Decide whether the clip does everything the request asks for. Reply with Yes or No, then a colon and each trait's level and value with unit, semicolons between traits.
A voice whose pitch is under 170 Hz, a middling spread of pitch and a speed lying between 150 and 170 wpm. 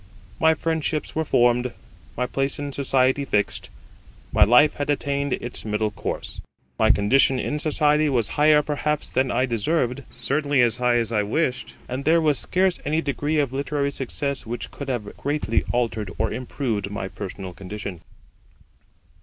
Yes: low, 135 Hz; average, 4.0 semitones; average, 160 wpm